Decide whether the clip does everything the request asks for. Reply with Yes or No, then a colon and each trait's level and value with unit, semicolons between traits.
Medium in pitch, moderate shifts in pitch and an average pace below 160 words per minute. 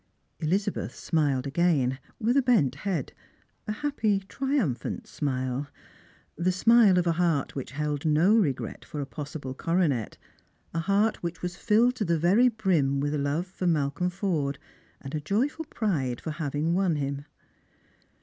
No: medium, 170 Hz; wide, 5.7 semitones; average, 145 wpm